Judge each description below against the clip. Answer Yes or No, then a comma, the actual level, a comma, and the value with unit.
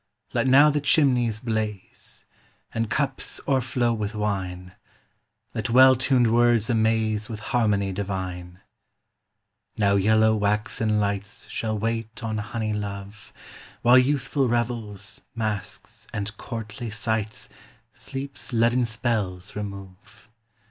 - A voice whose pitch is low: Yes, low, 110 Hz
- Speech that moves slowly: Yes, slow, 110 wpm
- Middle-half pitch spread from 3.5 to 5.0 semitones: No, average, 2.7 semitones